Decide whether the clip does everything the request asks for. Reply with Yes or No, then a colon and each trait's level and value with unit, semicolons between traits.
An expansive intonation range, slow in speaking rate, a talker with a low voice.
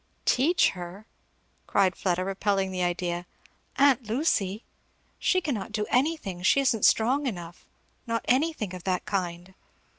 No: wide, 5.9 semitones; slow, 130 wpm; high, 200 Hz